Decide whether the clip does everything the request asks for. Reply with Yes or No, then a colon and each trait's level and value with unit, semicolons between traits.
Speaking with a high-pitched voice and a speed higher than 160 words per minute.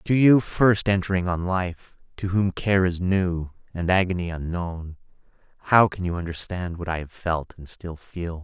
No: very low, 90 Hz; average, 180 wpm